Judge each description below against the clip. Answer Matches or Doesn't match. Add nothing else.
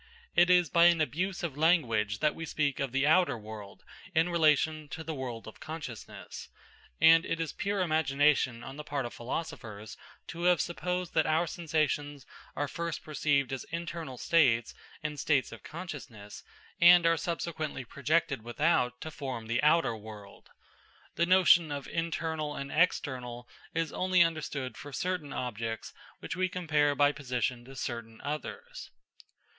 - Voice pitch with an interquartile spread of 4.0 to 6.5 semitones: Matches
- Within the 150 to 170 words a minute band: Matches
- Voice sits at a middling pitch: Matches